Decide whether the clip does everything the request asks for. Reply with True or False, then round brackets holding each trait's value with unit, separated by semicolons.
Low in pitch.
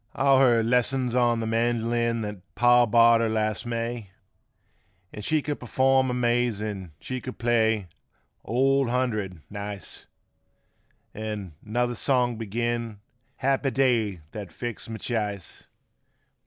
True (115 Hz)